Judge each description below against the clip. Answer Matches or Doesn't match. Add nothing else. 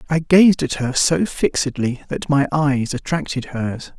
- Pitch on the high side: Doesn't match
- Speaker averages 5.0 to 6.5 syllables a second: Doesn't match